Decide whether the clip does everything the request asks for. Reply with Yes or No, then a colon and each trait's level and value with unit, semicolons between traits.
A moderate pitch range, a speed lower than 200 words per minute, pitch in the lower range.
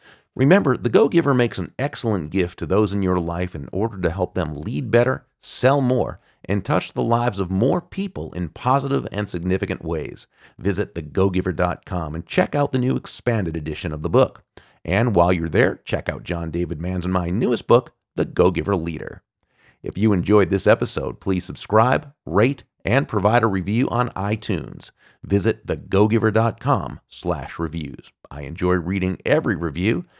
Yes: average, 4.9 semitones; average, 165 wpm; very low, 95 Hz